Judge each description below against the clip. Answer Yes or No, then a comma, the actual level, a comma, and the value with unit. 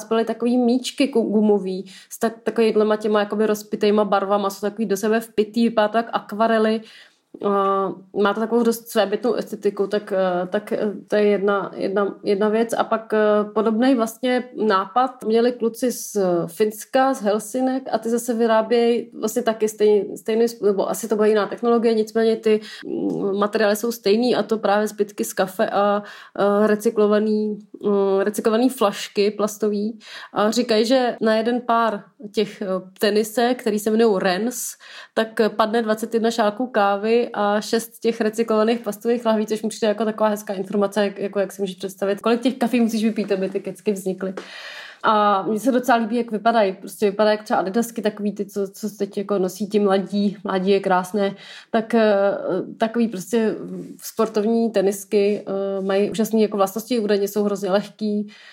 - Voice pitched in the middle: No, high, 215 Hz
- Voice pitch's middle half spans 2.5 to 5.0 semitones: No, narrow, 2.0 semitones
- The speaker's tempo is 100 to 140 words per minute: No, average, 160 wpm